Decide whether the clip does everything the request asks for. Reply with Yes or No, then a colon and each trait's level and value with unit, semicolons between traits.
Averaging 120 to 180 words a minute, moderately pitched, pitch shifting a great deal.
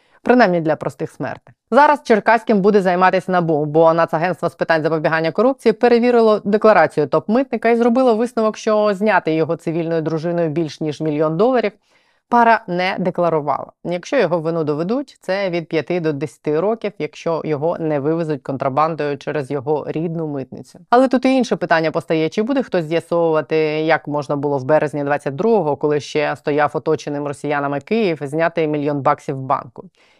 Yes: fast, 155 wpm; medium, 165 Hz; wide, 5.7 semitones